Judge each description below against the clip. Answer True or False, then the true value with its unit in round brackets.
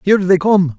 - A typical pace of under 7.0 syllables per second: True (5.8 syllables/s)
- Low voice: False (185 Hz)